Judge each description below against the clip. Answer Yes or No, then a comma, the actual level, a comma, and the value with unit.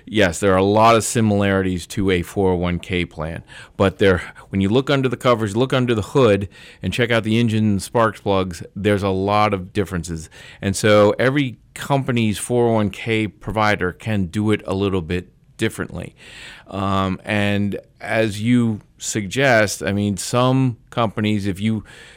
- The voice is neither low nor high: No, low, 105 Hz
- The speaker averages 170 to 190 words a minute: No, average, 160 wpm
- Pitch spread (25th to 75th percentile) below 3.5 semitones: Yes, average, 3.1 semitones